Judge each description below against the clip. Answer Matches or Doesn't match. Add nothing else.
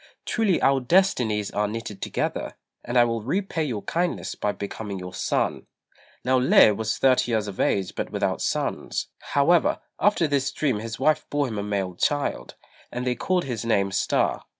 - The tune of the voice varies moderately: Doesn't match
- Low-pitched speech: Matches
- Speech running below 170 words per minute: Doesn't match